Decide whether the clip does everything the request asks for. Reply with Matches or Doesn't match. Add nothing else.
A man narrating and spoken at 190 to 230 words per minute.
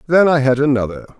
Matches